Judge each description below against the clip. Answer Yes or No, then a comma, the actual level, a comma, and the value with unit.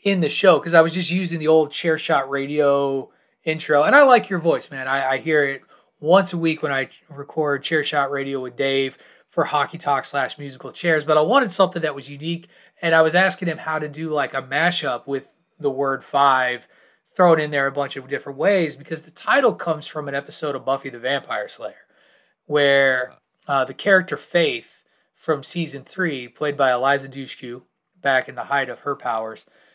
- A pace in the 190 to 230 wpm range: Yes, fast, 205 wpm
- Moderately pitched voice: Yes, medium, 150 Hz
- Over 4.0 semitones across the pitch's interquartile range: No, average, 3.4 semitones